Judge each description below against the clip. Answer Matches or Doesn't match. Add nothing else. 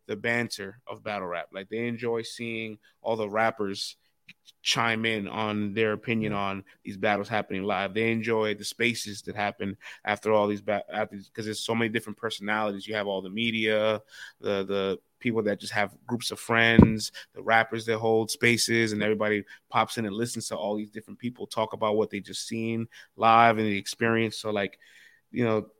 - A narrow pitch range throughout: Matches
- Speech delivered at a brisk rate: Doesn't match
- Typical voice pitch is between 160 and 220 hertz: Doesn't match